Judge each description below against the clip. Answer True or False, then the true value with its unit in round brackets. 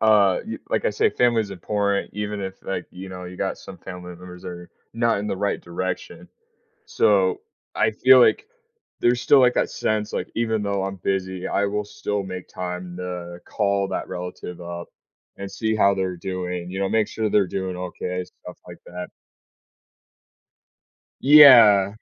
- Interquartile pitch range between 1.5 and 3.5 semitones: True (2.6 semitones)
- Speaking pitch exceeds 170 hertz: False (95 Hz)